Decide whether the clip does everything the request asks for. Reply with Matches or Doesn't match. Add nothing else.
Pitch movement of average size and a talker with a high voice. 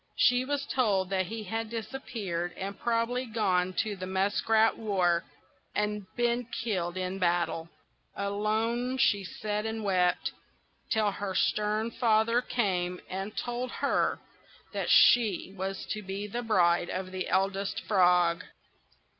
Matches